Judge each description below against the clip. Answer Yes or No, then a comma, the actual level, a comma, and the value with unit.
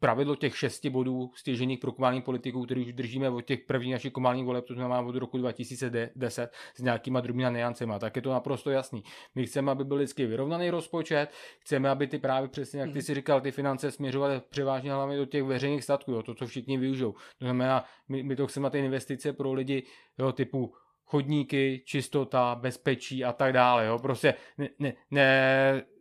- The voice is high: No, low, 135 Hz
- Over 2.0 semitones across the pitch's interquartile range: No, narrow, 1.7 semitones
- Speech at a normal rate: No, fast, 195 wpm